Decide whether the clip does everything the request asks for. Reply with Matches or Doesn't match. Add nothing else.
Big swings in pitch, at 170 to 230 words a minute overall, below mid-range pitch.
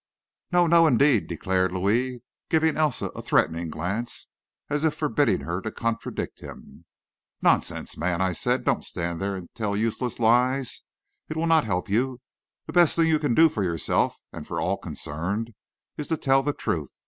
Matches